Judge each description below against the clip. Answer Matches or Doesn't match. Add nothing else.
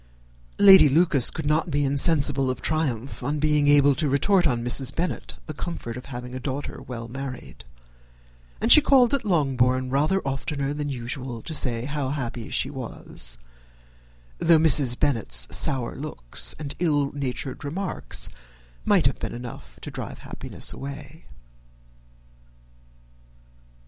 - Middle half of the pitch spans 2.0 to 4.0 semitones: Matches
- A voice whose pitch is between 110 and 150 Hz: Matches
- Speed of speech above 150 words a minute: Doesn't match